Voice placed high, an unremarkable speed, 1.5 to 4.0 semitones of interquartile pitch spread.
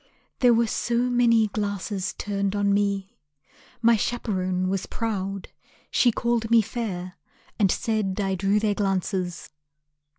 No: high, 205 Hz; slow, 130 wpm; average, 2.9 semitones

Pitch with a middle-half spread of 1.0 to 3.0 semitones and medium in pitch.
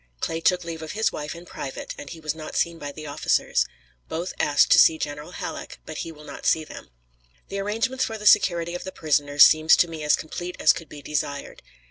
Yes: average, 2.7 semitones; medium, 160 Hz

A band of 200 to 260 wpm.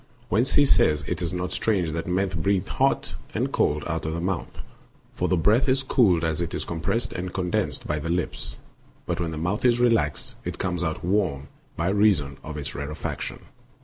Yes: fast, 205 wpm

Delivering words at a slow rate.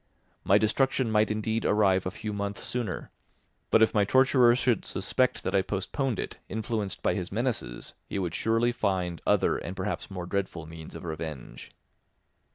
No: average, 165 wpm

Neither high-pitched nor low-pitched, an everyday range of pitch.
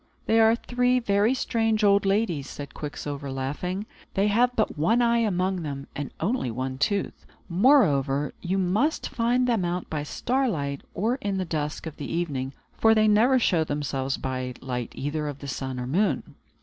No: medium, 180 Hz; wide, 7.8 semitones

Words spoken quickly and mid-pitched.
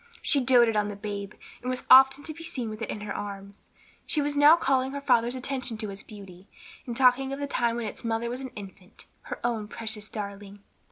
No: fast, 225 wpm; high, 235 Hz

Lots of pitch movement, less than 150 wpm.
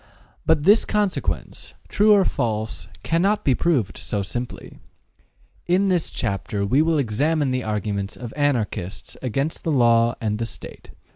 Yes: wide, 7.1 semitones; average, 140 wpm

